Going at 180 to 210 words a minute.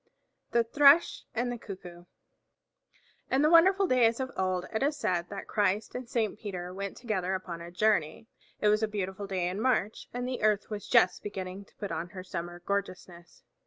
Yes: average, 190 wpm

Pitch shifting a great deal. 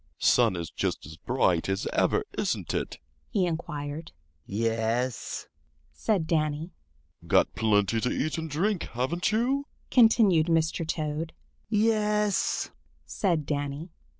Yes: wide, 7.1 semitones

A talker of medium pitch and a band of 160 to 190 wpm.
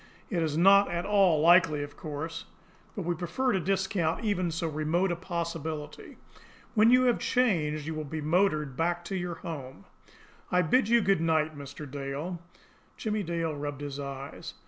Yes: medium, 165 Hz; average, 170 wpm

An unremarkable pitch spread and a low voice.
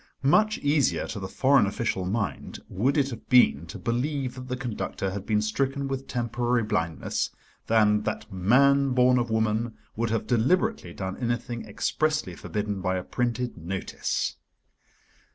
Yes: average, 3.9 semitones; low, 120 Hz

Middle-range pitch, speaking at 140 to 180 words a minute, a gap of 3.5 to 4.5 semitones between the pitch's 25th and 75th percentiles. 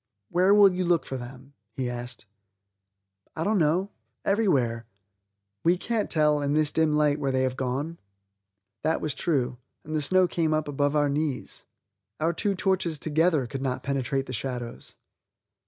Yes: medium, 150 Hz; average, 165 wpm; average, 4.2 semitones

